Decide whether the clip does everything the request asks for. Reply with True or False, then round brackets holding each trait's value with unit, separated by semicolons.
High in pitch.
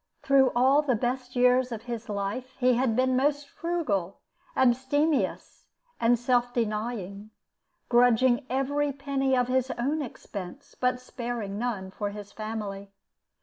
True (245 Hz)